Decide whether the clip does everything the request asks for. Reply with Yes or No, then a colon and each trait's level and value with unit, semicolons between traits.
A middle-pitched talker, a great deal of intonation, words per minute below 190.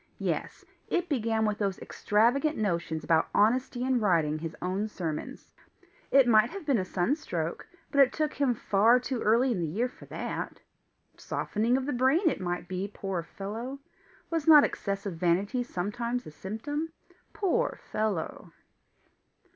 No: high, 220 Hz; wide, 5.9 semitones; average, 155 wpm